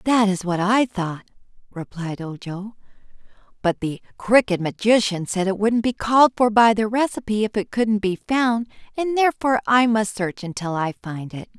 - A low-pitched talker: No, high, 210 Hz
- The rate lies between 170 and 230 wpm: Yes, average, 175 wpm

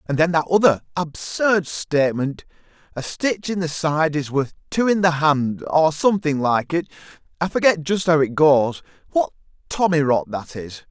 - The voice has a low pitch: No, medium, 160 Hz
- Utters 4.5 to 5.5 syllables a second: Yes, 4.6 syllables/s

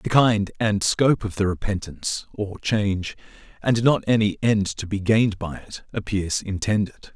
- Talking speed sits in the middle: Yes, average, 170 wpm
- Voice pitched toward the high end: No, low, 105 Hz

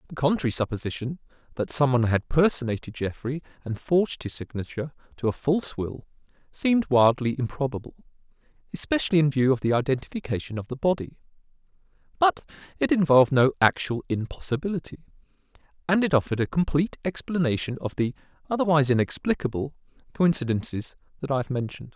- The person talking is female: No, male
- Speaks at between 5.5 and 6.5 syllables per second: Yes, 6.4 syllables/s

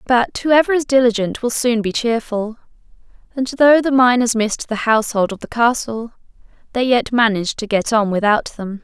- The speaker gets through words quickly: No, average, 175 wpm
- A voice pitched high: Yes, high, 235 Hz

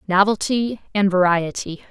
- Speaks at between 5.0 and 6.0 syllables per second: No, 4.4 syllables/s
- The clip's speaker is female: Yes, female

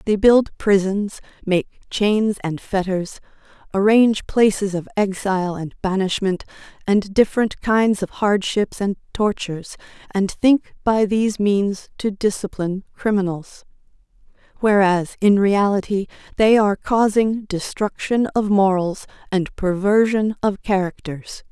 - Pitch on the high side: Yes, high, 200 Hz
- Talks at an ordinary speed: No, slow, 115 wpm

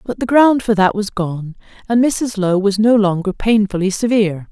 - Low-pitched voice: No, high, 210 Hz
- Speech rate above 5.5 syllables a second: No, 4.9 syllables/s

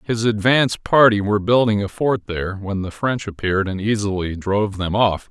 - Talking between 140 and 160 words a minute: No, average, 190 wpm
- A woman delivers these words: No, male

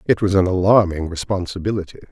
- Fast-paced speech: No, average, 140 wpm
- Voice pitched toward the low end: Yes, very low, 95 Hz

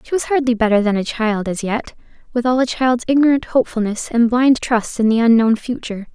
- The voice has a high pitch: Yes, high, 235 Hz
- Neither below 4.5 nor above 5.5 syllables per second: No, 5.7 syllables/s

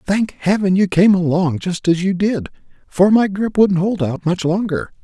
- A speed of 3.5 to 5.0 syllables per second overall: Yes, 4.8 syllables/s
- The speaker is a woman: No, male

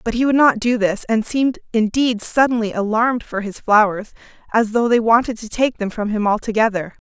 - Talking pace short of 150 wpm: No, fast, 205 wpm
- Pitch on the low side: No, high, 225 Hz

